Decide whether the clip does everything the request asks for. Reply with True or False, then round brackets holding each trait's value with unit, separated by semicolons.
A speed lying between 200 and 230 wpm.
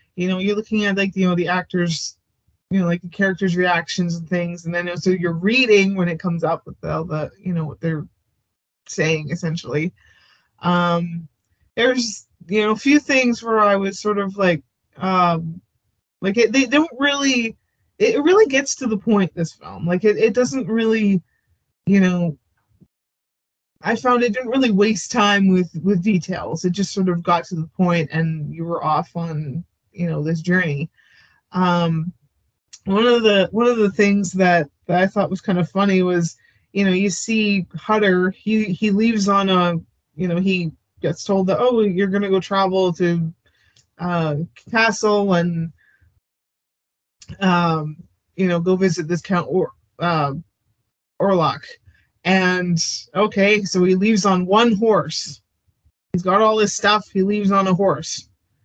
False (170 wpm)